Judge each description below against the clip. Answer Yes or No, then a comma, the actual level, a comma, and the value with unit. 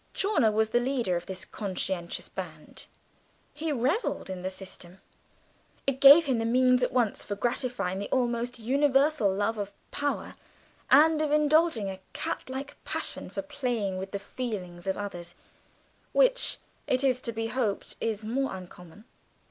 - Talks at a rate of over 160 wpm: No, average, 155 wpm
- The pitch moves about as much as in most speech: No, wide, 5.8 semitones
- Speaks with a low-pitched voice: No, high, 235 Hz